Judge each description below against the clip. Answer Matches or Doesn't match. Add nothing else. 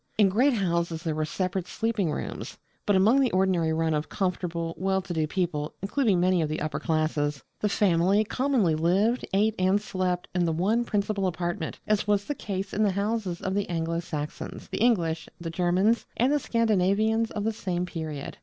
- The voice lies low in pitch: Doesn't match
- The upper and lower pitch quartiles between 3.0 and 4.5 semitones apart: Matches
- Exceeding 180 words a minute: Matches